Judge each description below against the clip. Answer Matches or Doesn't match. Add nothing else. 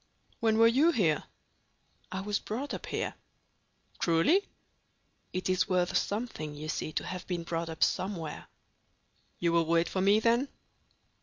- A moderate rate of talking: Matches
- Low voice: Doesn't match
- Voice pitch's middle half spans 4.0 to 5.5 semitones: Matches